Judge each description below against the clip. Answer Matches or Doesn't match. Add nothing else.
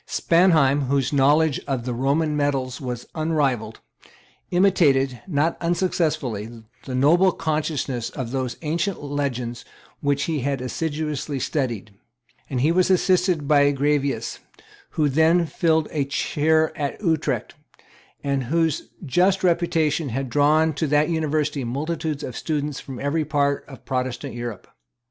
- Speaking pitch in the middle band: Matches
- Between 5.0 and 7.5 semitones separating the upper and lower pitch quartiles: Doesn't match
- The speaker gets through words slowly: Matches